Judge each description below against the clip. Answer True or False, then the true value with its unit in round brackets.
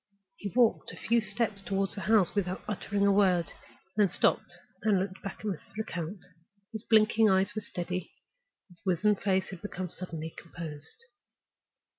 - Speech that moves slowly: False (165 wpm)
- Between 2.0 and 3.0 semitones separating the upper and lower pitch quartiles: True (2.6 semitones)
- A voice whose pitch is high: True (195 Hz)